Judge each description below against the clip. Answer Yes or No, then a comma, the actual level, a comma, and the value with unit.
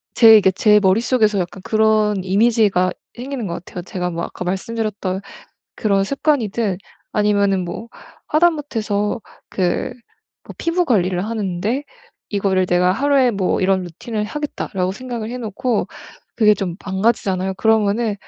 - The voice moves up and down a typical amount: Yes, average, 3.5 semitones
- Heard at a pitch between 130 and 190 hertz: No, high, 210 Hz